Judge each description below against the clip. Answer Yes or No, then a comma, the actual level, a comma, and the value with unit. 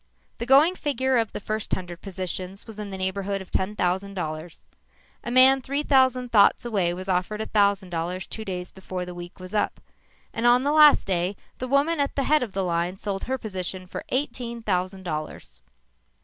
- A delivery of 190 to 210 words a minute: Yes, average, 200 wpm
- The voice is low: No, high, 200 Hz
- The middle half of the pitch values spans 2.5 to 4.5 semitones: No, average, 5.3 semitones